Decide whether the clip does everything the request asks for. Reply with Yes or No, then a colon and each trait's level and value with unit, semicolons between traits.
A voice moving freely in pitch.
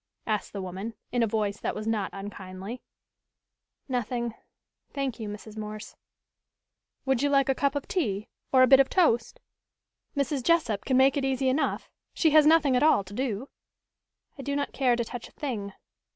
No: average, 4.5 semitones